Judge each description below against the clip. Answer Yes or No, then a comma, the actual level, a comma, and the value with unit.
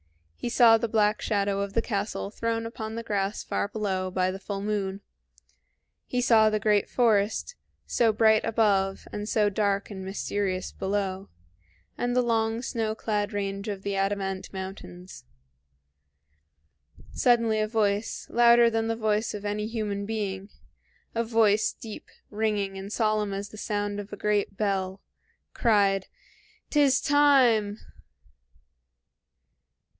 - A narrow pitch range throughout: Yes, narrow, 2.1 semitones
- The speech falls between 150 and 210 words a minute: No, average, 140 wpm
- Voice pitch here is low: No, high, 210 Hz